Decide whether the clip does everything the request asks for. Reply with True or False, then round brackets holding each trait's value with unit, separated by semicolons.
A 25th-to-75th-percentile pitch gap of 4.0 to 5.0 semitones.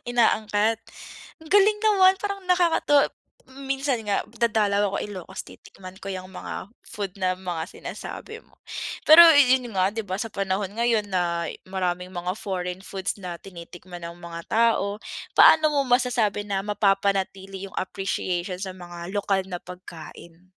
True (4.3 semitones)